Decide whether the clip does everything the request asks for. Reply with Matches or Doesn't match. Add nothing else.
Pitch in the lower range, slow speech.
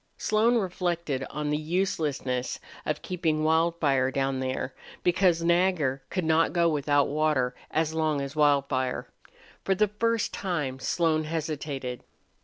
Doesn't match